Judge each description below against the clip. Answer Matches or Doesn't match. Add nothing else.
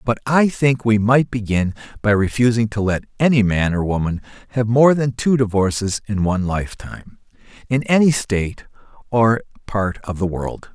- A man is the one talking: Matches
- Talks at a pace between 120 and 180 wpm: Matches